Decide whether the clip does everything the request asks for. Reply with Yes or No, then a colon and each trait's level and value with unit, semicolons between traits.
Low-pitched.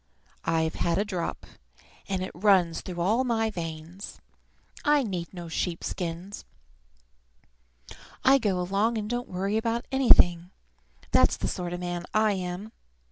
No: medium, 185 Hz